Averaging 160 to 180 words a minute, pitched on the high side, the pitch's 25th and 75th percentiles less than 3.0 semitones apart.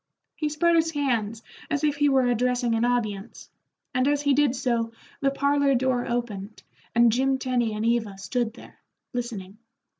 No: average, 170 wpm; high, 245 Hz; average, 3.4 semitones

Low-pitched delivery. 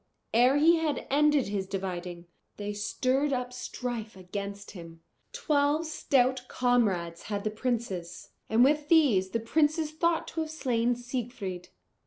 No: high, 245 Hz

